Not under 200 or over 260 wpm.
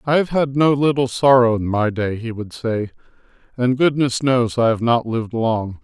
Yes: fast, 205 wpm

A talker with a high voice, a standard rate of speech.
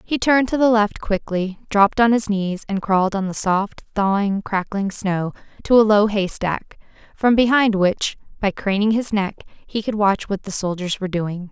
Yes: high, 205 Hz; average, 195 wpm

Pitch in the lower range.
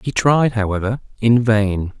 Yes: low, 110 Hz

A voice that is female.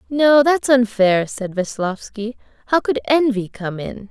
Yes: female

